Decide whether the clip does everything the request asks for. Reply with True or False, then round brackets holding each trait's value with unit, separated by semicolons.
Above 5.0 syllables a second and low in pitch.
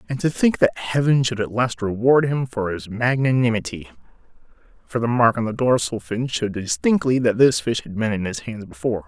True (5.5 syllables/s; 115 Hz)